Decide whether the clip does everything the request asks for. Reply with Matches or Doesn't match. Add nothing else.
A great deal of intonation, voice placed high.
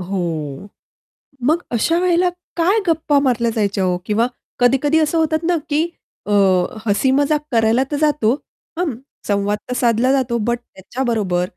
Matches